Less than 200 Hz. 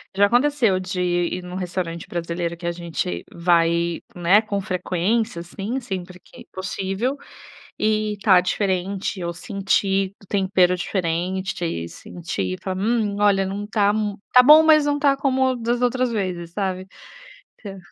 Yes: high, 190 Hz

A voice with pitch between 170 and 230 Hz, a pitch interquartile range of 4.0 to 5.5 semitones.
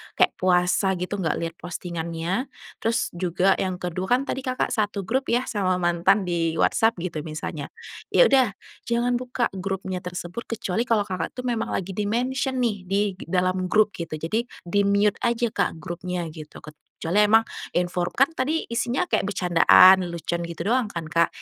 Yes: high, 190 Hz; average, 4.9 semitones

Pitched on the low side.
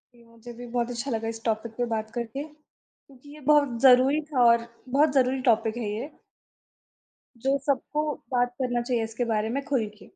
No: high, 245 Hz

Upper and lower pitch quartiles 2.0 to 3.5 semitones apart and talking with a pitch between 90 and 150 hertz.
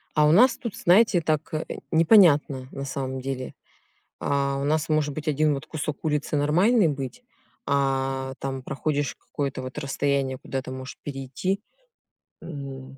Yes: average, 2.7 semitones; medium, 140 Hz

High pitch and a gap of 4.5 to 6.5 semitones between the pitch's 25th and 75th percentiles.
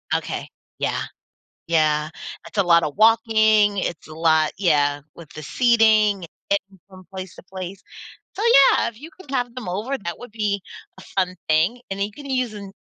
Yes: high, 200 Hz; average, 4.9 semitones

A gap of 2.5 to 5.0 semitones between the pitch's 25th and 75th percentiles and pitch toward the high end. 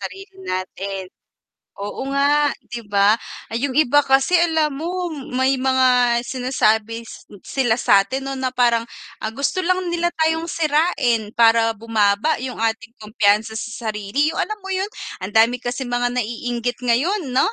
Yes: average, 4.5 semitones; very high, 250 Hz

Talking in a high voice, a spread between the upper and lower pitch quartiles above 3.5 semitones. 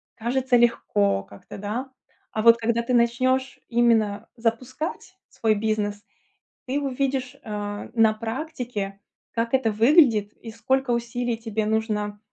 No: high, 230 Hz; average, 2.8 semitones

